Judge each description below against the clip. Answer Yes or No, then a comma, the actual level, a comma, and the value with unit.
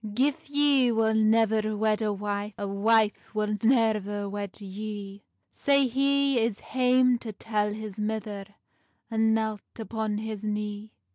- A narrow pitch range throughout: Yes, narrow, 1.7 semitones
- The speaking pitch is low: No, high, 215 Hz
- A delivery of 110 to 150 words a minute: Yes, average, 140 wpm